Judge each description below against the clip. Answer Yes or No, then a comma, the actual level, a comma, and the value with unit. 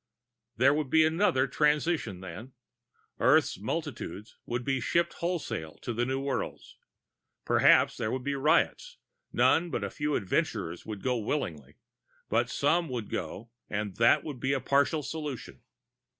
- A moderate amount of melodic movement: Yes, average, 5.0 semitones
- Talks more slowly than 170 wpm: Yes, average, 150 wpm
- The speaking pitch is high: No, low, 130 Hz